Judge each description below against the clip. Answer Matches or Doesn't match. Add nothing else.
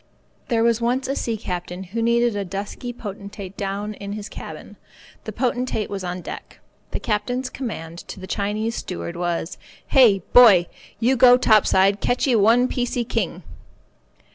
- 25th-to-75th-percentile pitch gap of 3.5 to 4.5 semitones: Matches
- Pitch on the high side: Matches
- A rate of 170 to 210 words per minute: Doesn't match